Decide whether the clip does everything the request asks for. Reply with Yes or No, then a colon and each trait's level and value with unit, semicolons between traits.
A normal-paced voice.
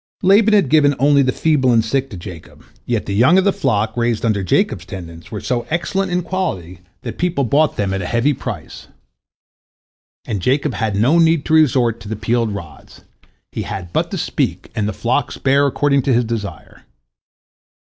Yes: average, 190 wpm